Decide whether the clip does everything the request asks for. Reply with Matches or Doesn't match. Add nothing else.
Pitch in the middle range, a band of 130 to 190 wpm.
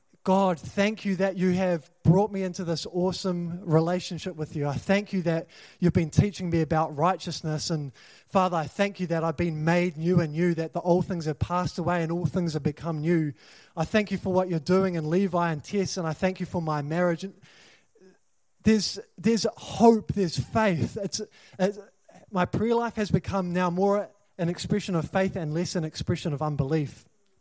Doesn't match